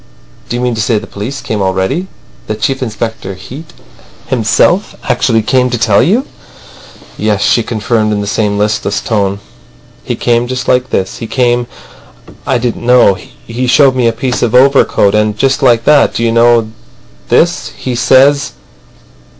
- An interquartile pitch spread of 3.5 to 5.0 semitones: No, average, 3.1 semitones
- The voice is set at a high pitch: No, low, 120 Hz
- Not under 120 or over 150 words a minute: No, average, 165 wpm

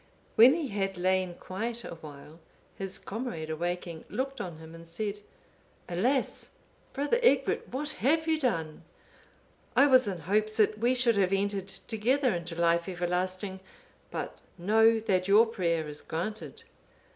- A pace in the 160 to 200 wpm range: No, average, 145 wpm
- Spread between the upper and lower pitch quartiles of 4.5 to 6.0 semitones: Yes, average, 5.3 semitones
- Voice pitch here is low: No, high, 195 Hz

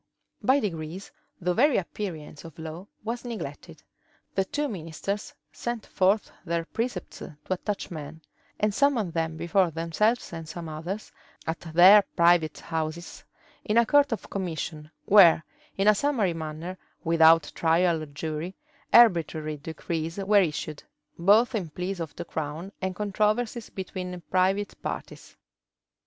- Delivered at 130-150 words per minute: Yes, average, 140 wpm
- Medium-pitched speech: Yes, medium, 180 Hz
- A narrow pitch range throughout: No, average, 4.3 semitones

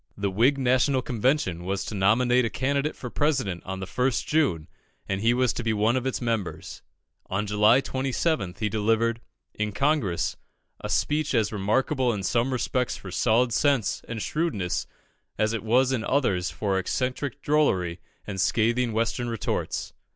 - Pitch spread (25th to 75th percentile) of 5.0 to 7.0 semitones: No, average, 4.2 semitones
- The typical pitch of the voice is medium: No, low, 115 Hz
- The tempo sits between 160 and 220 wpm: Yes, average, 165 wpm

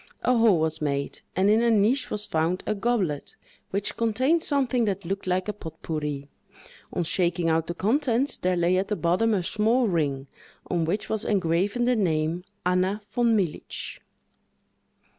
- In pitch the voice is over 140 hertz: Yes, high, 190 Hz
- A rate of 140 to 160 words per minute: No, average, 170 wpm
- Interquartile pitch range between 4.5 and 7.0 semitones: Yes, average, 5.1 semitones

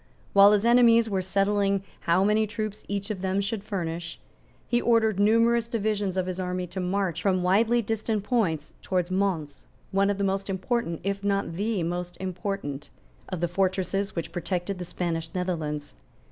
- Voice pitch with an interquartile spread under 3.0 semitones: Yes, narrow, 2.5 semitones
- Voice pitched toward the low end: No, high, 195 Hz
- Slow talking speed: No, average, 170 wpm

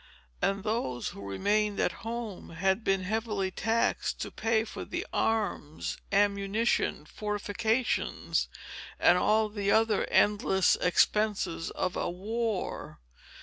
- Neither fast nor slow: No, slow, 115 wpm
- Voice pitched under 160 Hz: No, high, 205 Hz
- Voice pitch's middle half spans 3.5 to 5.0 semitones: No, narrow, 2.6 semitones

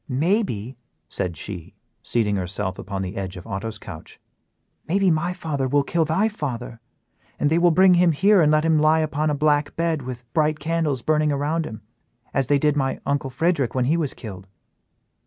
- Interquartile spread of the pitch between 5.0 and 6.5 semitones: Yes, wide, 5.4 semitones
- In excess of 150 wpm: Yes, average, 190 wpm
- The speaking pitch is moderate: Yes, medium, 145 Hz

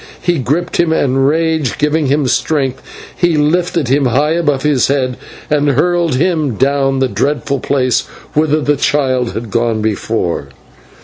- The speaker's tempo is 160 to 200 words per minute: No, average, 150 wpm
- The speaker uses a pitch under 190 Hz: Yes, medium, 140 Hz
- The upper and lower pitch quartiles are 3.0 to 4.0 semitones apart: Yes, average, 3.3 semitones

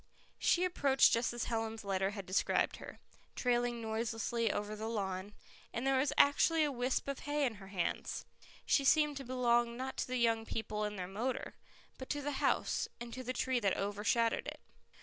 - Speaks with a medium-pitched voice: No, high, 235 Hz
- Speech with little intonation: No, average, 3.7 semitones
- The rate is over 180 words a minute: Yes, average, 190 wpm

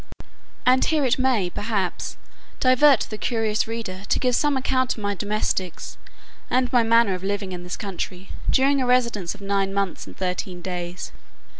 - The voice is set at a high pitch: Yes, high, 210 Hz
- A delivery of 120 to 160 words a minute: No, average, 170 wpm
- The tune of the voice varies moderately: Yes, average, 5.0 semitones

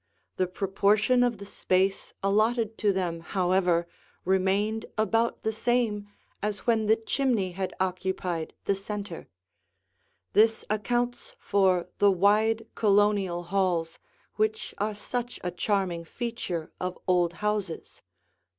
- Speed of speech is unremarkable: No, slow, 120 wpm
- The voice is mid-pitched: No, high, 200 Hz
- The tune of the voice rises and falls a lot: No, average, 3.0 semitones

